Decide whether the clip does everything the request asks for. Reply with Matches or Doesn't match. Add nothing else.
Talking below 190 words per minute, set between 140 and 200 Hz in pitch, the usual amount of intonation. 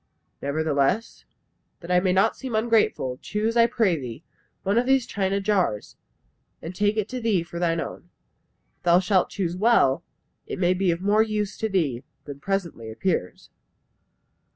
Matches